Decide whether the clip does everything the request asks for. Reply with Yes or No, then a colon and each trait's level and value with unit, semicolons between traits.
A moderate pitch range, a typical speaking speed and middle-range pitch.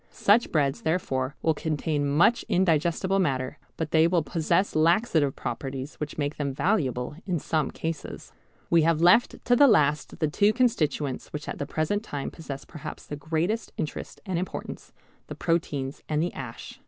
Yes: average, 3.5 semitones; average, 165 wpm; medium, 155 Hz